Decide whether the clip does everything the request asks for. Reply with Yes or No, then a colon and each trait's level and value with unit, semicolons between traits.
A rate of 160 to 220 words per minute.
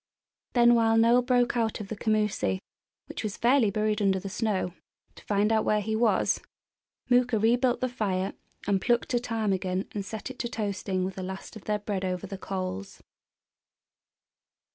Yes: average, 175 wpm